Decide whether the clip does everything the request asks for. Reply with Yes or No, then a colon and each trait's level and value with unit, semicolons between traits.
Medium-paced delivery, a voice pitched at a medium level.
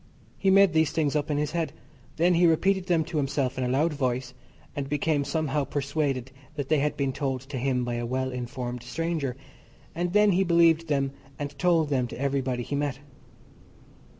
Yes: average, 195 wpm; medium, 145 Hz